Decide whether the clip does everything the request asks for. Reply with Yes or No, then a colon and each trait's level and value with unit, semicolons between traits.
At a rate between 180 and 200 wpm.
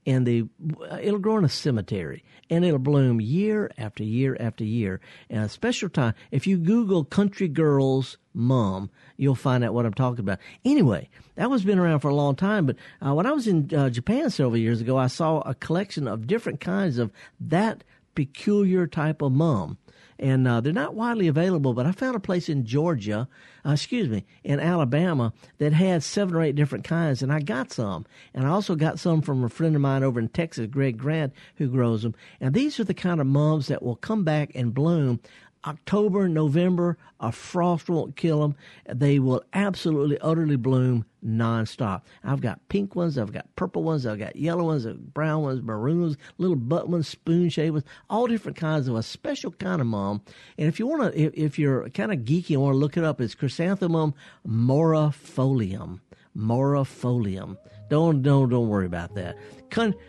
Yes: average, 195 wpm